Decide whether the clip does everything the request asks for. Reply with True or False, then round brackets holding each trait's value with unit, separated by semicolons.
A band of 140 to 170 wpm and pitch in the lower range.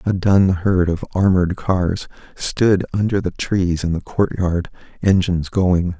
True (160 wpm; 90 Hz)